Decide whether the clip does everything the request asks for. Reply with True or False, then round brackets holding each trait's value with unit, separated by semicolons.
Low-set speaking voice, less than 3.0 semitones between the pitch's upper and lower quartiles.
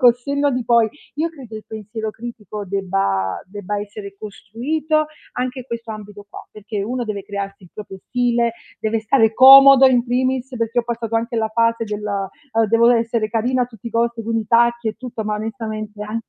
False (225 Hz; 2.4 semitones)